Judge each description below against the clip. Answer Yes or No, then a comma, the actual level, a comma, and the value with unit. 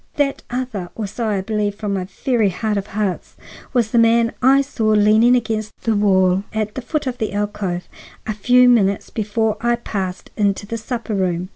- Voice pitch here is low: No, high, 215 Hz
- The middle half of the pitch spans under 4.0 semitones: Yes, average, 2.8 semitones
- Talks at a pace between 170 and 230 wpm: Yes, average, 190 wpm